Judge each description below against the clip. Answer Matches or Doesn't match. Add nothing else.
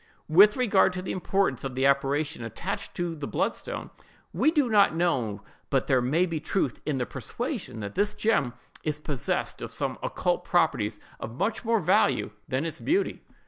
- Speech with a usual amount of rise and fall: Doesn't match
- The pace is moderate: Matches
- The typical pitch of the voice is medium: Matches